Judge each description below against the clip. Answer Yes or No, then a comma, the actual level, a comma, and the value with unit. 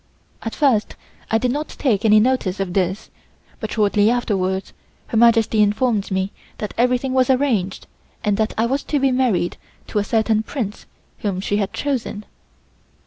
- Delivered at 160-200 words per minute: Yes, average, 165 wpm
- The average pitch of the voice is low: No, high, 220 Hz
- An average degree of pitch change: Yes, average, 3.7 semitones